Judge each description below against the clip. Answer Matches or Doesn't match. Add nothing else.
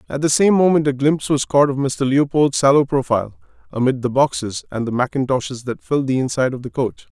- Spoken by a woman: Doesn't match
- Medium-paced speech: Doesn't match